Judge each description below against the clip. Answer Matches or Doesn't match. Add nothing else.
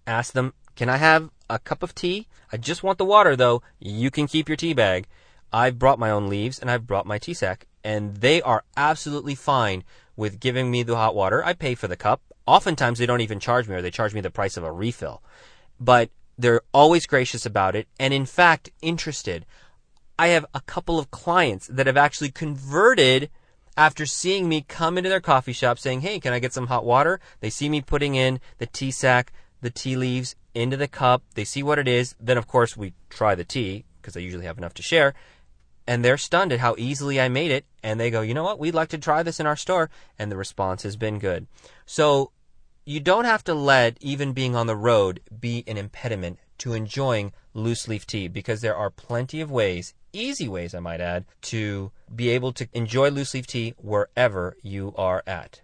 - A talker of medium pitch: Doesn't match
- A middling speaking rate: Doesn't match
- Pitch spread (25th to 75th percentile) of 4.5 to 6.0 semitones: Matches